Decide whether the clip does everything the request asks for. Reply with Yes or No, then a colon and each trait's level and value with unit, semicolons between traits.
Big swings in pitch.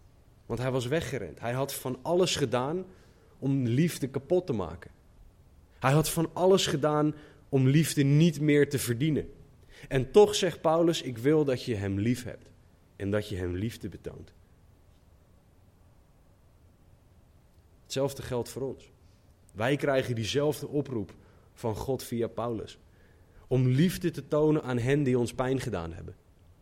Yes: wide, 7.1 semitones